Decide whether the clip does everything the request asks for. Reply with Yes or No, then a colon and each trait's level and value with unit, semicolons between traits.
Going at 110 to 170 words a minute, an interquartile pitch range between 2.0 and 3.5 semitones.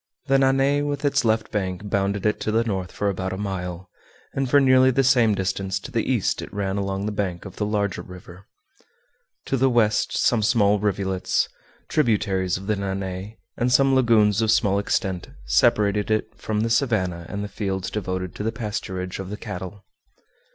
No: average, 185 wpm; average, 3.0 semitones